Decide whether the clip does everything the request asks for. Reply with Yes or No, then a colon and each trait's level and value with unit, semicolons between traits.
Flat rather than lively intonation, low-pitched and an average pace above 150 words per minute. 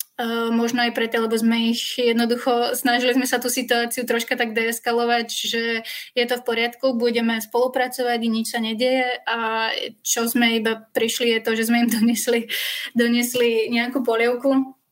No: narrow, 1.2 semitones; high, 235 Hz; fast, 165 wpm